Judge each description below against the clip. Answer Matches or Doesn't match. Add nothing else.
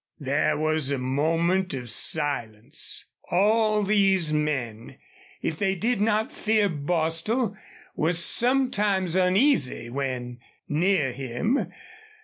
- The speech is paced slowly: Matches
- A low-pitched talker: Doesn't match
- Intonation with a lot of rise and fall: Matches